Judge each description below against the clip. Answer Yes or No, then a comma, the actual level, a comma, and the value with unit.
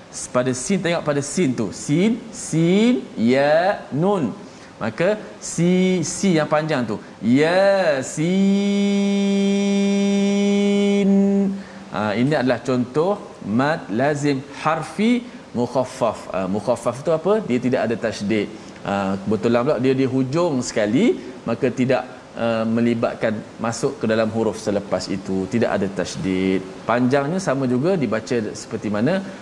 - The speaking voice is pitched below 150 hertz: Yes, medium, 140 Hz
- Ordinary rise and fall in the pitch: No, wide, 8.9 semitones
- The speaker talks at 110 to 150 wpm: Yes, average, 120 wpm